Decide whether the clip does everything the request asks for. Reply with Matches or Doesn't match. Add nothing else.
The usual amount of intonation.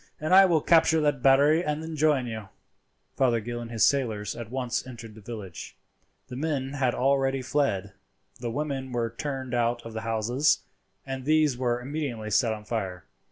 Matches